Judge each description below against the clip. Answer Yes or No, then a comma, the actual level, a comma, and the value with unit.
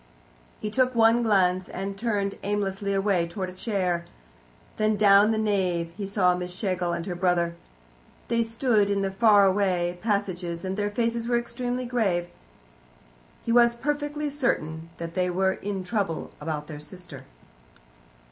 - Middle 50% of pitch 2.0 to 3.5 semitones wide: No, average, 3.9 semitones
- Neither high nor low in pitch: No, high, 195 Hz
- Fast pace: No, average, 155 wpm